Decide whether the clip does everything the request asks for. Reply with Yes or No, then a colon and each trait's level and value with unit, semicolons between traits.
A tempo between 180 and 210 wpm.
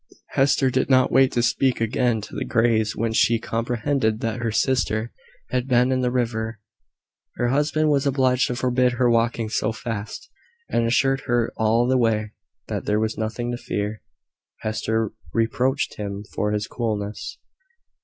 No: average, 165 wpm